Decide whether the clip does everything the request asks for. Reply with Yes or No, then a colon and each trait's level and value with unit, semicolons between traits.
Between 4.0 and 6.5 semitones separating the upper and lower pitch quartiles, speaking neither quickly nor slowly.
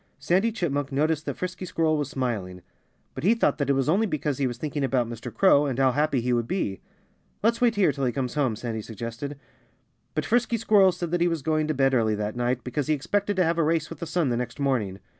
No: wide, 5.5 semitones; fast, 250 wpm